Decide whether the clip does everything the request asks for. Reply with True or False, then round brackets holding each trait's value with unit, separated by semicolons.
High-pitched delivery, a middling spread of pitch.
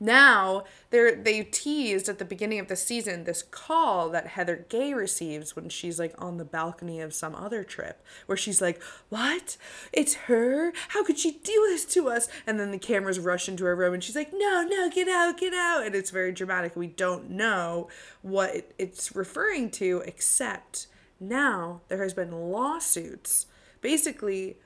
False (200 Hz; 8.0 semitones)